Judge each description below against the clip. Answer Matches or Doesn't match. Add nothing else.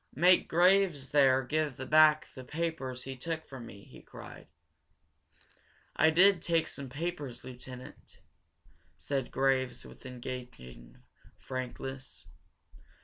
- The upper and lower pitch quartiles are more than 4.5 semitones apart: Doesn't match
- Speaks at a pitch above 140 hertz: Doesn't match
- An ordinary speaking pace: Doesn't match